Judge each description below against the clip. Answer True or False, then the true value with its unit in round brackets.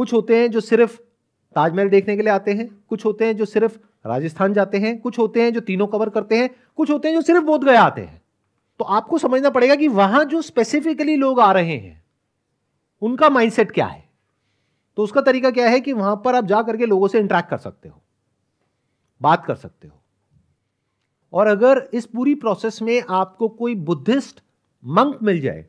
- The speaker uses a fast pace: True (200 wpm)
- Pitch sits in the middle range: False (225 Hz)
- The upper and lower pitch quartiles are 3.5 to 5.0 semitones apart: True (4.1 semitones)